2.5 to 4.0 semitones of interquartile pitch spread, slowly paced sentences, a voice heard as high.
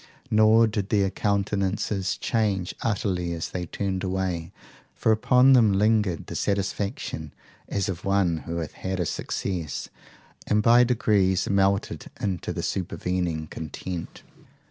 No: average, 3.0 semitones; slow, 130 wpm; very low, 95 Hz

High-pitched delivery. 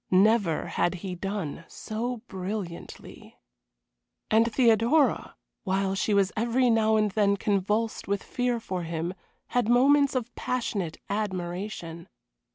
Yes: high, 210 Hz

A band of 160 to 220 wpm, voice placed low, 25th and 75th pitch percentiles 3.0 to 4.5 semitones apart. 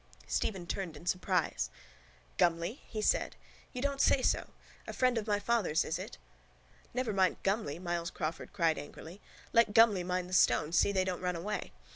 No: average, 175 wpm; medium, 185 Hz; average, 3.9 semitones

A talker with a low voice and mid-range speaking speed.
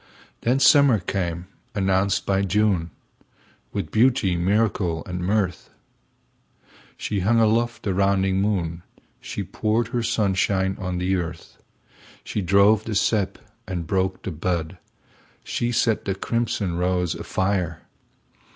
No: very low, 95 Hz; slow, 105 wpm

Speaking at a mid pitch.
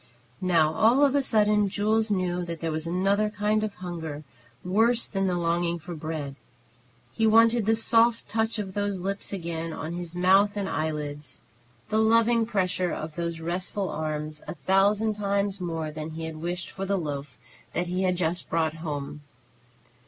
Yes: medium, 180 Hz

